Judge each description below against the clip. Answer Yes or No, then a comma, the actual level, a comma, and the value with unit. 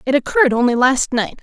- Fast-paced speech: Yes, fast, 210 wpm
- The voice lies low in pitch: No, very high, 260 Hz